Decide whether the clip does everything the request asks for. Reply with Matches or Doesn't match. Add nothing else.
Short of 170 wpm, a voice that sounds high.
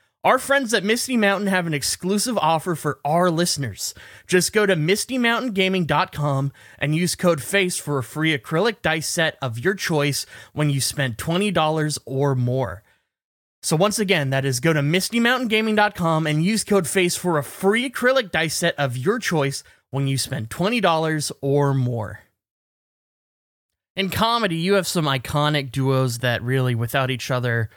Doesn't match